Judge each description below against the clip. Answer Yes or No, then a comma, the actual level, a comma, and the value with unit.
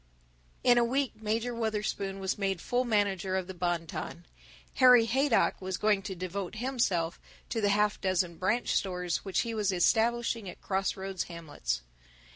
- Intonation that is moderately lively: Yes, average, 3.8 semitones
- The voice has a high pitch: Yes, high, 200 Hz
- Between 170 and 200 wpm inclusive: No, average, 160 wpm